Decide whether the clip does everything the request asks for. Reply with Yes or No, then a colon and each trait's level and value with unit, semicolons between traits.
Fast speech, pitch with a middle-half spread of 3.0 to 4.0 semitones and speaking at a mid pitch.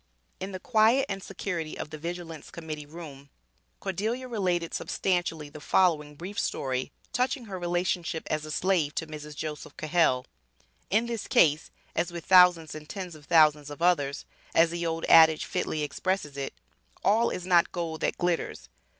No: average, 165 wpm; average, 3.4 semitones; medium, 170 Hz